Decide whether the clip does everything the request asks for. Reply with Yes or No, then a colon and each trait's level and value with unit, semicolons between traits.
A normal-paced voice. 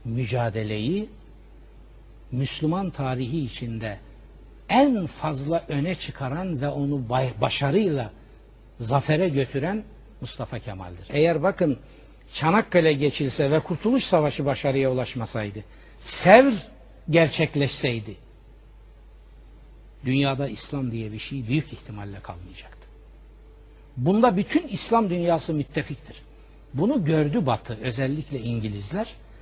No: slow, 90 wpm